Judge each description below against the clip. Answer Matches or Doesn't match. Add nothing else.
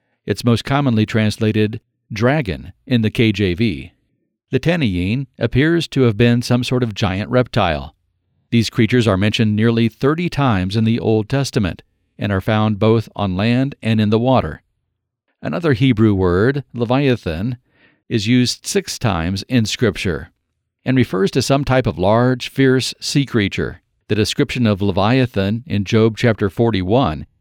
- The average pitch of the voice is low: Matches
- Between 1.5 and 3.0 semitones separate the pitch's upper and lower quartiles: Doesn't match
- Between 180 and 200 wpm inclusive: Doesn't match